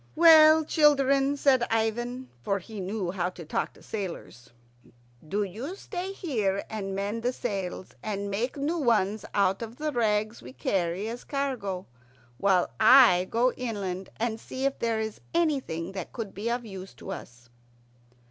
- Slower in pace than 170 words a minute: Yes, average, 160 wpm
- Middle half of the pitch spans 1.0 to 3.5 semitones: No, average, 5.1 semitones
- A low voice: No, high, 220 Hz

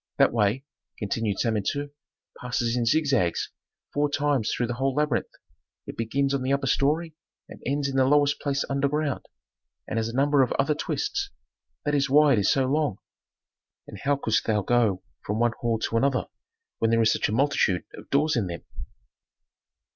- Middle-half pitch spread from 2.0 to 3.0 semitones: No, average, 4.0 semitones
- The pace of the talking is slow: No, average, 180 wpm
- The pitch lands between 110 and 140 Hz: Yes, low, 135 Hz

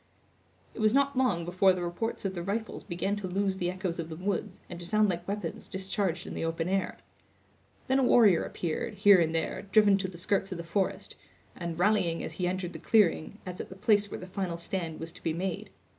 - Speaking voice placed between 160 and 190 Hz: Yes, medium, 185 Hz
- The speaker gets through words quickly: Yes, fast, 230 wpm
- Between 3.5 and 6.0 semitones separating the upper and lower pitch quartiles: No, average, 2.9 semitones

